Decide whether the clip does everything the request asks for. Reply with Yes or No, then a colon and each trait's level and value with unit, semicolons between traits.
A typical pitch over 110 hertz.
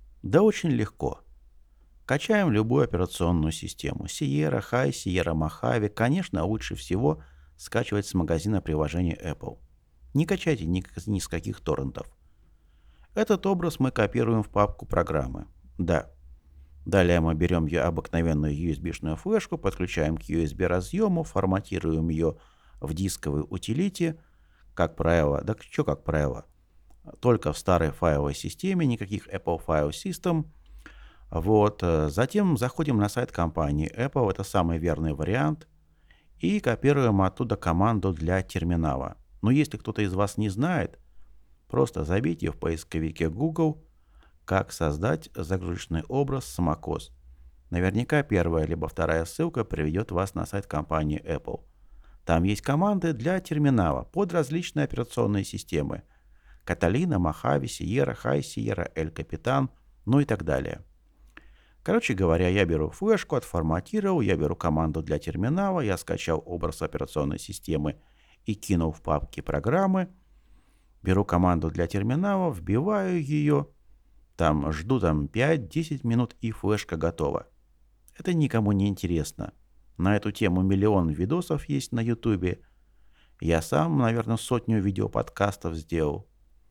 No: very low, 95 Hz